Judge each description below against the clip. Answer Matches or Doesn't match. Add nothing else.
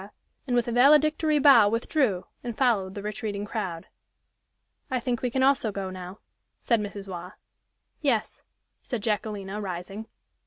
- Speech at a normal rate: Matches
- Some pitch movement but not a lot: Matches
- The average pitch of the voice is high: Matches